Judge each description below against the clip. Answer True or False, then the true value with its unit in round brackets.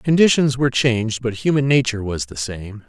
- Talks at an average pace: True (190 wpm)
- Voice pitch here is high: False (125 Hz)